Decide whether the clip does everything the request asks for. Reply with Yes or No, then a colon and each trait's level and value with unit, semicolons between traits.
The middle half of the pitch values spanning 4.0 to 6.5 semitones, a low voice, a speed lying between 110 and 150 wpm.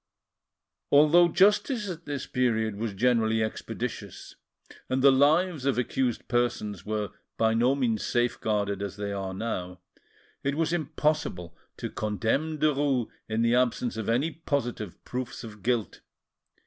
Yes: average, 4.9 semitones; low, 120 Hz; average, 140 wpm